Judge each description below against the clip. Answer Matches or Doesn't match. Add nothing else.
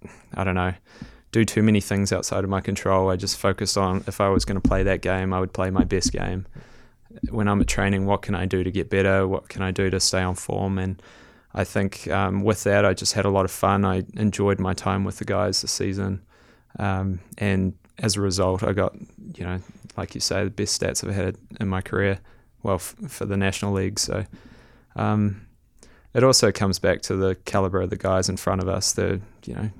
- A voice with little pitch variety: Matches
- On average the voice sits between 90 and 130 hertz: Matches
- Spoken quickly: Matches